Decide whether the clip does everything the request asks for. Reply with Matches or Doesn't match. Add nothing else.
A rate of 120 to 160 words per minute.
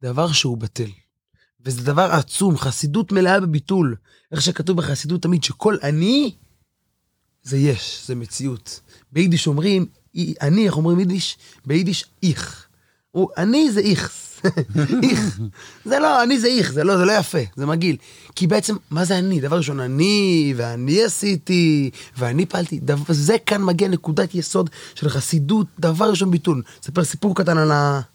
Matches